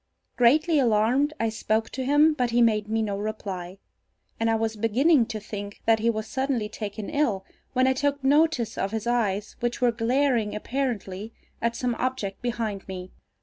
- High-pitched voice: Yes, high, 230 Hz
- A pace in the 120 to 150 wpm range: No, average, 180 wpm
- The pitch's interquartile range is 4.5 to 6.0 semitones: No, average, 3.5 semitones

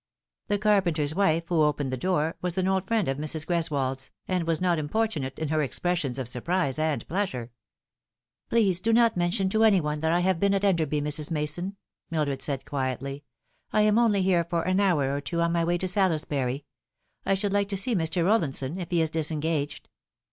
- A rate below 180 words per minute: No, fast, 205 wpm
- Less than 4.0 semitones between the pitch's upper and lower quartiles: No, average, 4.3 semitones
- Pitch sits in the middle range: Yes, medium, 170 Hz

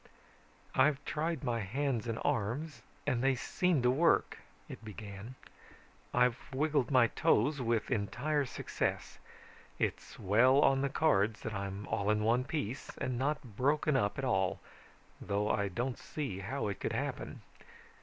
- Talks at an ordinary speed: Yes, average, 150 wpm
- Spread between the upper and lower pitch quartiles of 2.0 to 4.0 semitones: No, average, 4.7 semitones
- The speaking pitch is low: Yes, low, 125 Hz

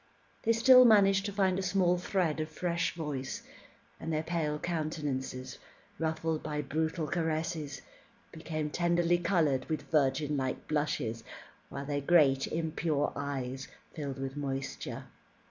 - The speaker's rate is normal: No, slow, 130 wpm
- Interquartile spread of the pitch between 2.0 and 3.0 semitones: No, average, 3.4 semitones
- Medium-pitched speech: Yes, medium, 155 Hz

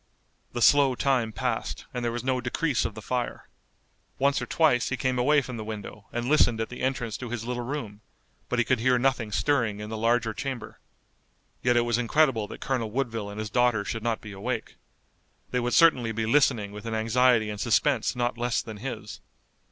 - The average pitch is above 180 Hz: No, low, 120 Hz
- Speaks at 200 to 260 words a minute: Yes, fast, 205 wpm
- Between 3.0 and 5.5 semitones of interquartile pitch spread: No, narrow, 2.5 semitones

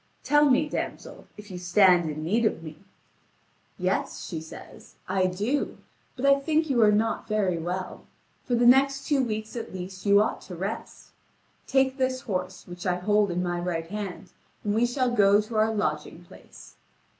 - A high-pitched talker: Yes, high, 210 Hz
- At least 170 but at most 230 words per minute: Yes, average, 180 wpm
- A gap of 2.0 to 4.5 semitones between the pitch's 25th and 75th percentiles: No, average, 5.2 semitones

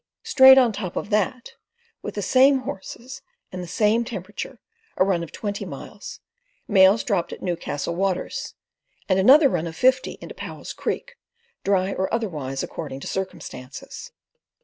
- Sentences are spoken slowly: No, average, 150 wpm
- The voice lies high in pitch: Yes, high, 195 Hz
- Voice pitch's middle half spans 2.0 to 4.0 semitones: No, average, 4.8 semitones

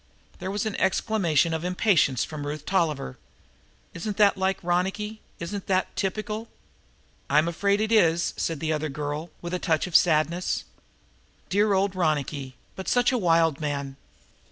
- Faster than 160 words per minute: No, average, 155 wpm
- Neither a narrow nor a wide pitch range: Yes, average, 4.4 semitones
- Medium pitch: Yes, medium, 175 Hz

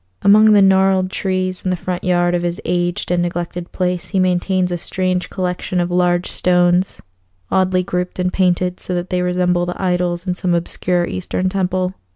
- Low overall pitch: No, medium, 180 Hz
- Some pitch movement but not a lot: No, narrow, 0.9 semitones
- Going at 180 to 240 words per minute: Yes, average, 185 wpm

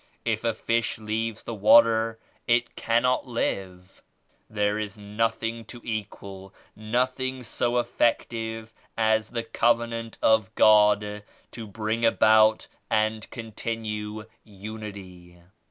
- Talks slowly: Yes, slow, 110 wpm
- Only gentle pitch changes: Yes, narrow, 1.6 semitones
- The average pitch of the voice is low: Yes, low, 110 Hz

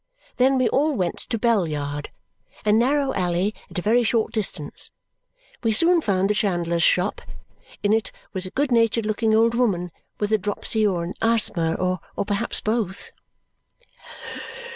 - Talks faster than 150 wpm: Yes, average, 160 wpm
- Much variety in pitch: No, average, 4.0 semitones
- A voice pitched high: Yes, high, 210 Hz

